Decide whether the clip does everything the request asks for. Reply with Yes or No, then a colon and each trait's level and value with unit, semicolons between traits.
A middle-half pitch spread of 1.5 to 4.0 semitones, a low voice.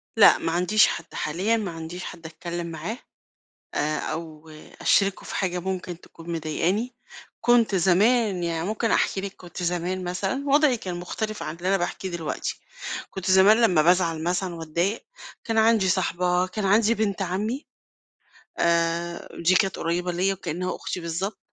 No: average, 2.9 semitones; medium, 180 Hz